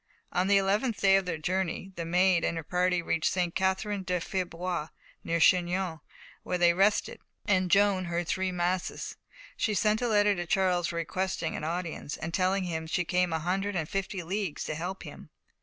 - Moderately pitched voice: Yes, medium, 180 Hz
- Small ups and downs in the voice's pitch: Yes, narrow, 2.1 semitones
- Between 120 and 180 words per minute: No, average, 190 wpm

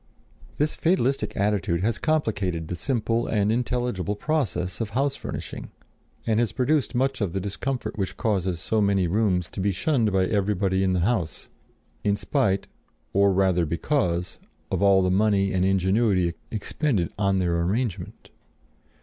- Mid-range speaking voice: No, low, 100 Hz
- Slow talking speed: No, average, 150 wpm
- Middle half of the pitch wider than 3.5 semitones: Yes, average, 3.9 semitones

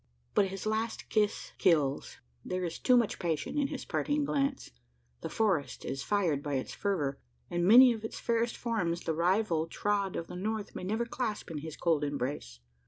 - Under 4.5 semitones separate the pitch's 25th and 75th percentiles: No, wide, 5.6 semitones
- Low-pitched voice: No, high, 195 Hz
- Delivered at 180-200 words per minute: Yes, average, 185 wpm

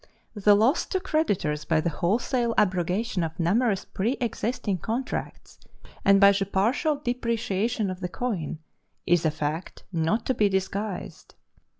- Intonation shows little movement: No, average, 4.9 semitones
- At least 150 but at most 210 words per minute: No, slow, 135 wpm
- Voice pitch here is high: Yes, high, 200 Hz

